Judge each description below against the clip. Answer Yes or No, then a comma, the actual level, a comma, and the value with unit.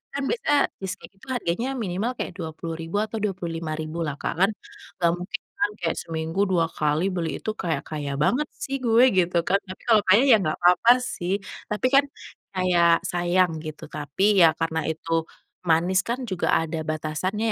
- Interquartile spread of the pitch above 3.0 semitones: Yes, average, 3.5 semitones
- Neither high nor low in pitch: Yes, medium, 175 Hz